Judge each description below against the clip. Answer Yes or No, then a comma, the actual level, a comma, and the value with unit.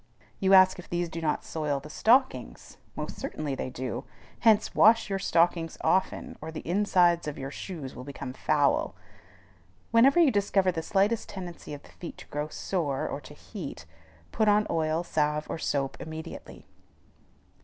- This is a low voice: No, medium, 170 Hz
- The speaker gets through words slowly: No, average, 165 wpm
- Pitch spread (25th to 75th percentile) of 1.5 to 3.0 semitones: No, average, 4.5 semitones